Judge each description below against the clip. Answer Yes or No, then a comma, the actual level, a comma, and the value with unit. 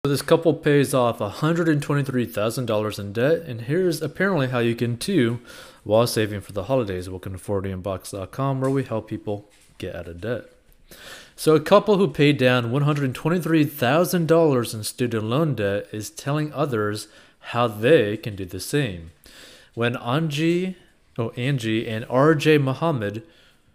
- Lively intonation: Yes, wide, 6.1 semitones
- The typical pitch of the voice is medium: No, low, 125 Hz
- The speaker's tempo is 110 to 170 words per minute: Yes, average, 150 wpm